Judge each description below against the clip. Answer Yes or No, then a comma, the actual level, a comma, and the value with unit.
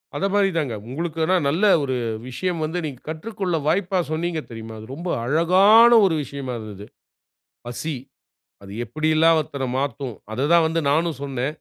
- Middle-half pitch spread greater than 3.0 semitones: Yes, average, 4.5 semitones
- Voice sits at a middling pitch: Yes, medium, 155 Hz